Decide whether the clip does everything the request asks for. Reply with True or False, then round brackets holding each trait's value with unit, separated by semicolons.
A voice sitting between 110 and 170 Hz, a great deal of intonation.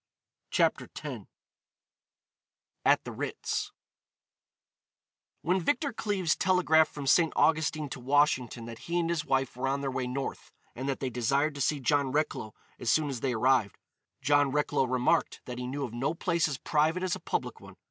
False (140 Hz; 3.7 semitones)